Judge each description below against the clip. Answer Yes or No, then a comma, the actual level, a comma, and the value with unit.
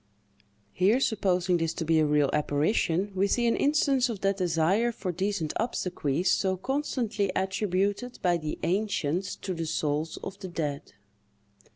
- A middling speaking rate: Yes, average, 155 wpm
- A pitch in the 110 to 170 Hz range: No, medium, 185 Hz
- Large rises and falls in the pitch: No, average, 4.1 semitones